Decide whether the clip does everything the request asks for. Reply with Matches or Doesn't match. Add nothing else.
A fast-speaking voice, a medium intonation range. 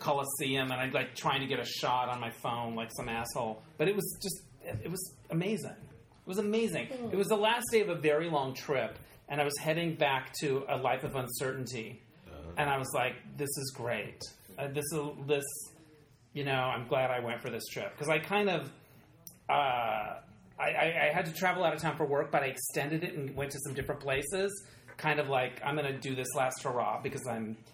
Matches